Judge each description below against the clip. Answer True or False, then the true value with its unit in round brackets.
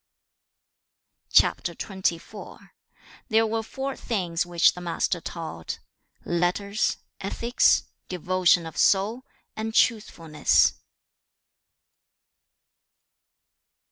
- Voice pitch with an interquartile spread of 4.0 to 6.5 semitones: True (4.4 semitones)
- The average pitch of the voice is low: False (185 Hz)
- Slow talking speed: True (75 wpm)